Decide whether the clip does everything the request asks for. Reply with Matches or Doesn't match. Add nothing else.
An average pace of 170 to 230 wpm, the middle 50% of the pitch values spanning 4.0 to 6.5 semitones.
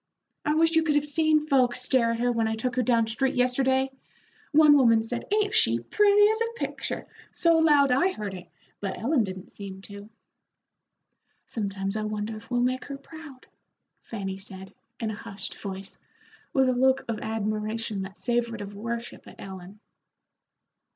Matches